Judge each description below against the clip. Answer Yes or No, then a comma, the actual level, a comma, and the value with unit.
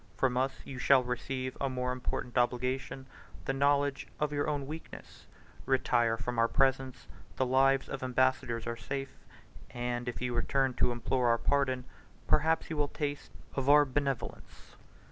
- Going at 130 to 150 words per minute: No, average, 160 wpm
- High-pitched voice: No, low, 130 Hz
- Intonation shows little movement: Yes, narrow, 1.9 semitones